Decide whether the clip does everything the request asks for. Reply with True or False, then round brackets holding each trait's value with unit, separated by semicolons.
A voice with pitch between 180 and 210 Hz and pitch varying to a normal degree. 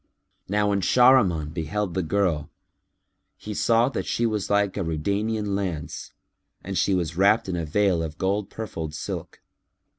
False (100 Hz; 4.0 semitones)